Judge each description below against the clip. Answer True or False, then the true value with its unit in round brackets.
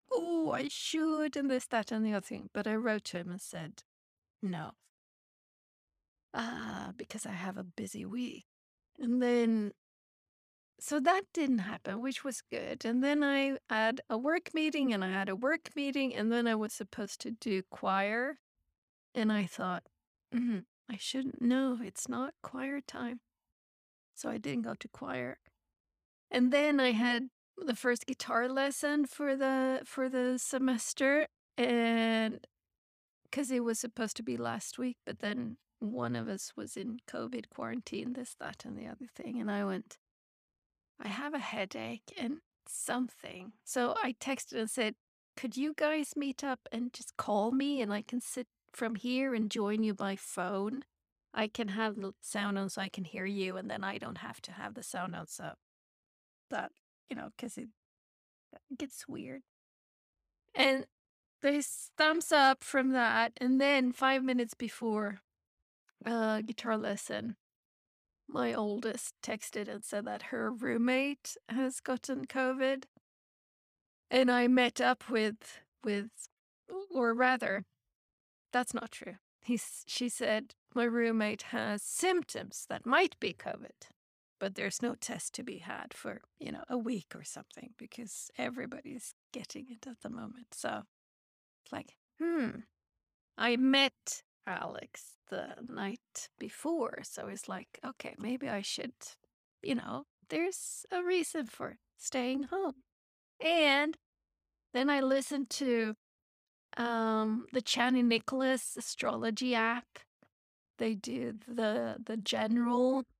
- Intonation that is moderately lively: True (3.5 semitones)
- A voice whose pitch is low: False (245 Hz)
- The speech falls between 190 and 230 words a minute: False (150 wpm)